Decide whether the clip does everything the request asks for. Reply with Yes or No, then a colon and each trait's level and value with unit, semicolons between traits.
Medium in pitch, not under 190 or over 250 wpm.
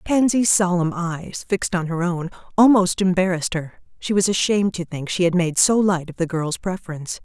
Yes: medium, 180 Hz; average, 200 wpm